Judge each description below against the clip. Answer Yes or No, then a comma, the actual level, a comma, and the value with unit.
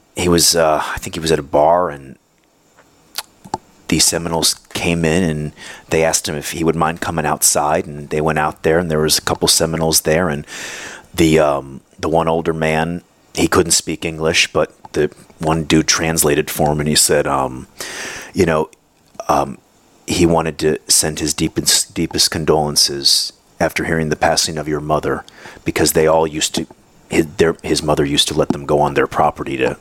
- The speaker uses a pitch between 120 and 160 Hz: No, very low, 80 Hz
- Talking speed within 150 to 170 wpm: No, average, 185 wpm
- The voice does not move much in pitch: Yes, narrow, 1.4 semitones